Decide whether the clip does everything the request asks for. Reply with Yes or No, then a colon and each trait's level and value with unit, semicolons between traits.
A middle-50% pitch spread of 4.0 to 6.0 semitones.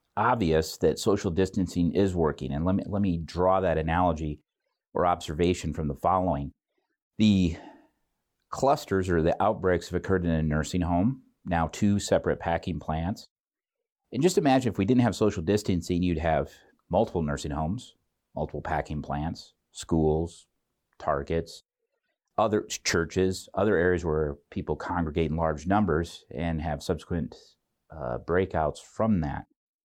No: average, 3.3 semitones